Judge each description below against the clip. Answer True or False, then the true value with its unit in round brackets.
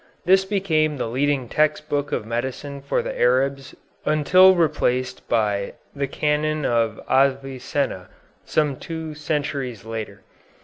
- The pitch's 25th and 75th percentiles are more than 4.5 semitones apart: False (3.6 semitones)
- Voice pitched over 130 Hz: True (140 Hz)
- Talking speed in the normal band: False (125 wpm)